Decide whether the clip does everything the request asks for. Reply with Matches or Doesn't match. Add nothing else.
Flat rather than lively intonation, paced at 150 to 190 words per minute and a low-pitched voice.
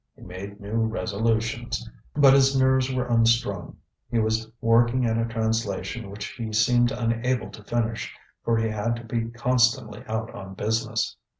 Matches